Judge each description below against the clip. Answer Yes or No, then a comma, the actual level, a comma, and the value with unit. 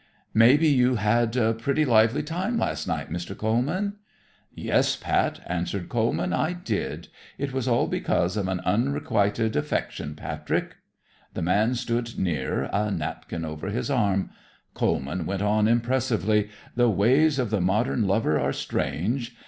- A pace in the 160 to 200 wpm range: No, average, 150 wpm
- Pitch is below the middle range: Yes, low, 110 Hz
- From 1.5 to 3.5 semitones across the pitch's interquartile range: No, average, 4.7 semitones